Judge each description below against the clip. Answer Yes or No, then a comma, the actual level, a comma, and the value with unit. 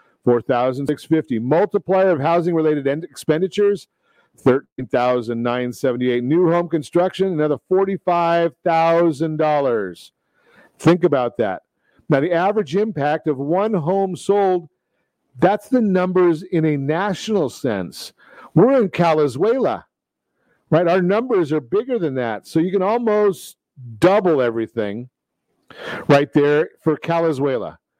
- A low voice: No, medium, 165 Hz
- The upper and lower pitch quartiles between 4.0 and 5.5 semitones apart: Yes, average, 4.6 semitones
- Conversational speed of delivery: No, slow, 105 wpm